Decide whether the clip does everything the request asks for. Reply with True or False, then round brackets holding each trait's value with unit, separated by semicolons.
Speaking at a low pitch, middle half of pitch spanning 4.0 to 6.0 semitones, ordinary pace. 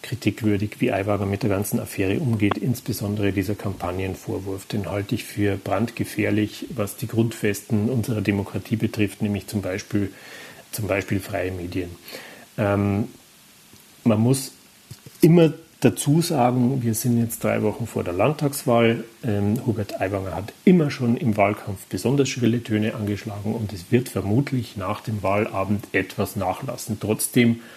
False (110 Hz; 2.9 semitones; 140 wpm)